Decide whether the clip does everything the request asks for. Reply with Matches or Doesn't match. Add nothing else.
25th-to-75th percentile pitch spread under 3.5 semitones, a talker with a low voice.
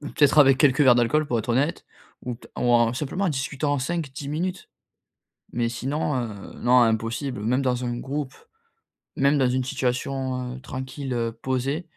Matches